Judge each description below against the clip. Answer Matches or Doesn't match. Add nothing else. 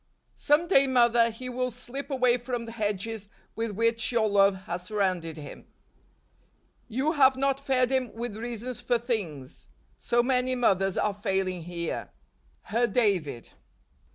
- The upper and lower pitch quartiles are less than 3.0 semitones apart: Doesn't match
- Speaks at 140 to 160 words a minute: Matches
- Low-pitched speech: Doesn't match